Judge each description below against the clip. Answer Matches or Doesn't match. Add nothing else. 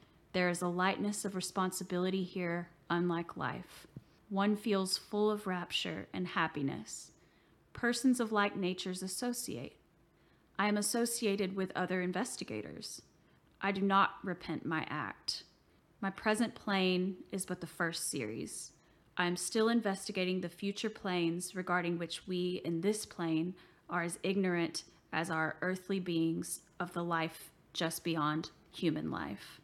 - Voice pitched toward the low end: Doesn't match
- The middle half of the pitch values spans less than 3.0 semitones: Matches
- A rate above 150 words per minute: Doesn't match